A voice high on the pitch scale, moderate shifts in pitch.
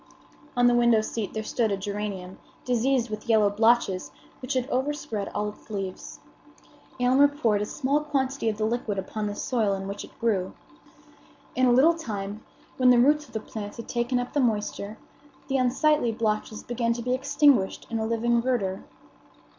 Yes: high, 230 Hz; average, 3.5 semitones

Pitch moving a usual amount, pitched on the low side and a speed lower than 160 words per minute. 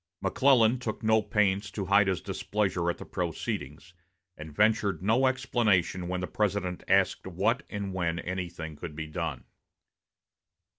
Yes: average, 3.7 semitones; very low, 95 Hz; average, 145 wpm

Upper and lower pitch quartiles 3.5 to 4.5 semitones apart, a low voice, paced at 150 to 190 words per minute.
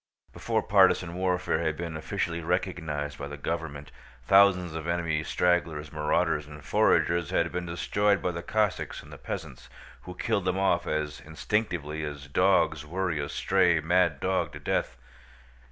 No: average, 3.0 semitones; very low, 85 Hz; average, 155 wpm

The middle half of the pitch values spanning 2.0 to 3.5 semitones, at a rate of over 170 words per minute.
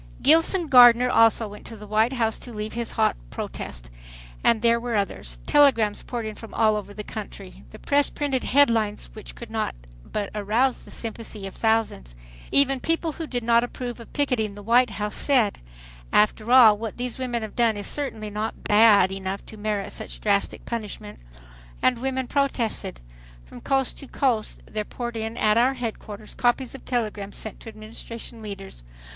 Yes: average, 3.0 semitones; average, 180 wpm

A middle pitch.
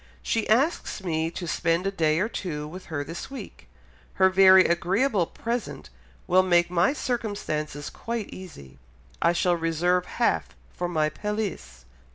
Yes: medium, 180 Hz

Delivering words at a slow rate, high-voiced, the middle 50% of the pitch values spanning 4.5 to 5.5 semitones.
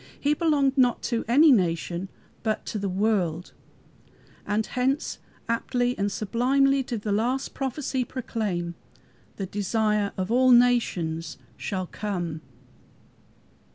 Yes: slow, 120 wpm; high, 220 Hz; average, 4.9 semitones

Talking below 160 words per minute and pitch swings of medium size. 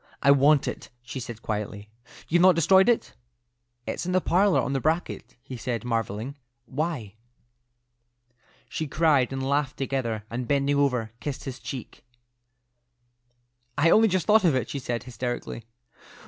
Yes: average, 150 wpm; average, 4.8 semitones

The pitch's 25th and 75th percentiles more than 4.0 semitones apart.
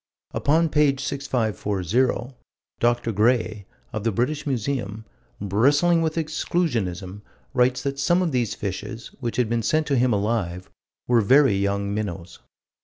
Yes: wide, 5.4 semitones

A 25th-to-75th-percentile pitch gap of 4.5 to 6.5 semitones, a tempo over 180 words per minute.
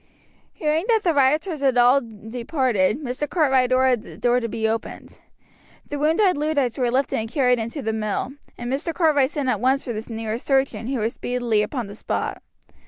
No: average, 3.8 semitones; average, 190 wpm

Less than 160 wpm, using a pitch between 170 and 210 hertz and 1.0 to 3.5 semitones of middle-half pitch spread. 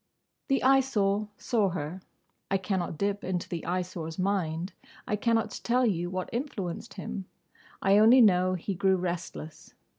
Yes: average, 145 wpm; high, 190 Hz; average, 3.1 semitones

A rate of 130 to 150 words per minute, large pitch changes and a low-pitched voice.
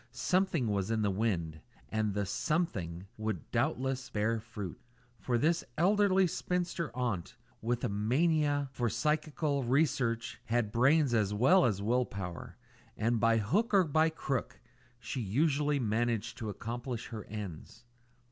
Yes: average, 140 wpm; wide, 5.8 semitones; low, 120 Hz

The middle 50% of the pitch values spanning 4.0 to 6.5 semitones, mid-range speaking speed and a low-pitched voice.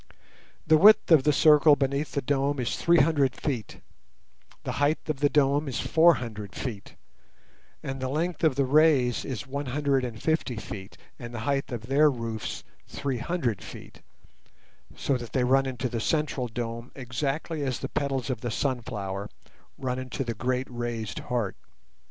No: average, 3.3 semitones; average, 170 wpm; low, 130 Hz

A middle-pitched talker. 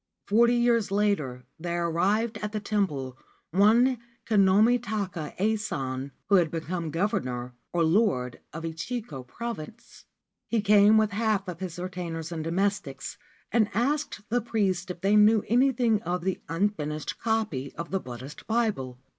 No: high, 195 Hz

